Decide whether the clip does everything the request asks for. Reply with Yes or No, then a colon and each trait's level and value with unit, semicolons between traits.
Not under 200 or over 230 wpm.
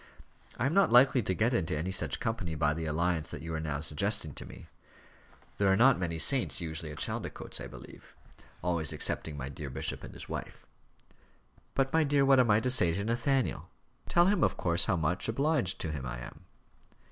Yes: fast, 205 wpm